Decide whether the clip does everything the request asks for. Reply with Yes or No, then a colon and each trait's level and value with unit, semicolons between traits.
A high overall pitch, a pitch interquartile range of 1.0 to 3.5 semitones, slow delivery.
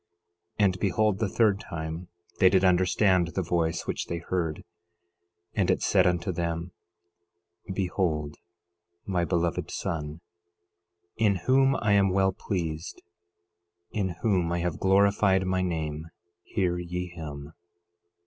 No: very low, 90 Hz; narrow, 2.6 semitones; slow, 130 wpm